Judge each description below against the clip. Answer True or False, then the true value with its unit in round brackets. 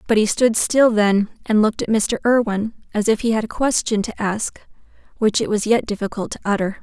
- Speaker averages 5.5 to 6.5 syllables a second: True (5.7 syllables/s)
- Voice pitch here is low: False (215 Hz)